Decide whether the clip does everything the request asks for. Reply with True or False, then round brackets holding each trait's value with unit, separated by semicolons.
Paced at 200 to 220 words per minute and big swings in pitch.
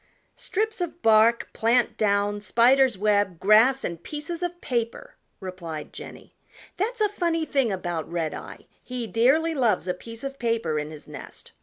False (155 wpm; 7.1 semitones)